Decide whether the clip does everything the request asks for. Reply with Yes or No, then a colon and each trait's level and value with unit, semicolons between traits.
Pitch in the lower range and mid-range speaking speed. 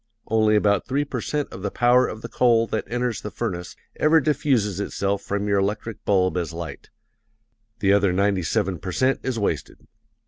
Yes: low, 105 Hz; average, 185 wpm